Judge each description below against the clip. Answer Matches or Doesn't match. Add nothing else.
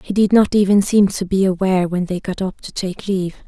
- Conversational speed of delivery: Doesn't match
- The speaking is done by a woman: Matches